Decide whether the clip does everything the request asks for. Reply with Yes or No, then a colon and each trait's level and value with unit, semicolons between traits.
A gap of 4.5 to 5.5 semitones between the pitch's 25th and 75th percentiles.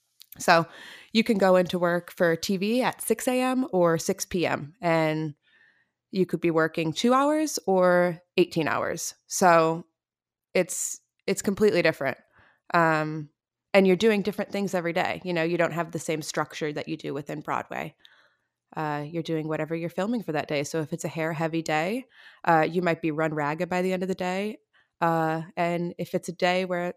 No: average, 2.7 semitones